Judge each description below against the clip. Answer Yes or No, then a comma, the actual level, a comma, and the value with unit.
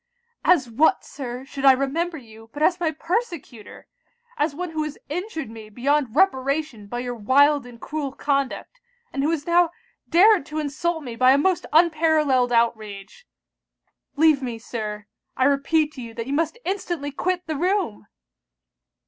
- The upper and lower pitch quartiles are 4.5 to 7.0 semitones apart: Yes, average, 5.0 semitones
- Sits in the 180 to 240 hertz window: No, very high, 285 Hz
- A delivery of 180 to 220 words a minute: No, average, 165 wpm